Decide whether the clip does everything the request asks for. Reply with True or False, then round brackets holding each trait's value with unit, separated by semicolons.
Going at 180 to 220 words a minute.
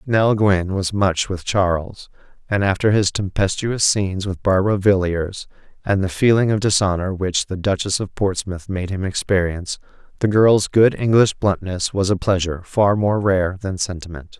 False (165 wpm)